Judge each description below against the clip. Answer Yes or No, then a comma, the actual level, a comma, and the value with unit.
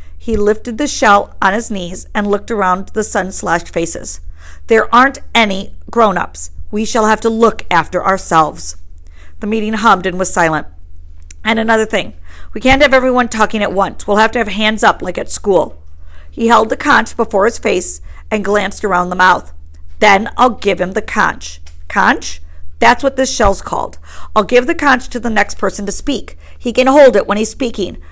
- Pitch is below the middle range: No, high, 200 Hz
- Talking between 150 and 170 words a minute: No, average, 195 wpm